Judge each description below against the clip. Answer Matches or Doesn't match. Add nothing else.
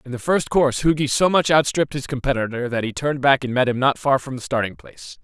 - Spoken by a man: Matches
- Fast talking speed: Matches